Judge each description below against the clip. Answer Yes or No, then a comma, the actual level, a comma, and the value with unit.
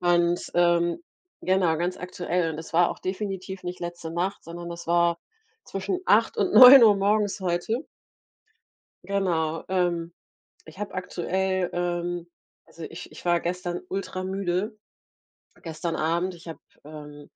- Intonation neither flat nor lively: No, narrow, 1.8 semitones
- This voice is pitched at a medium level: Yes, medium, 175 Hz